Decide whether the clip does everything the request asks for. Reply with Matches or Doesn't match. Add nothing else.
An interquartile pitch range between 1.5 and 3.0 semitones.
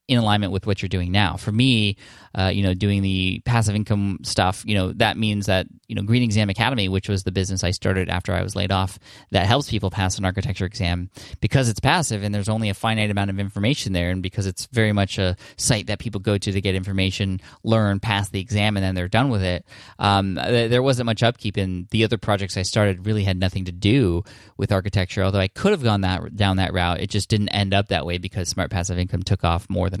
Matches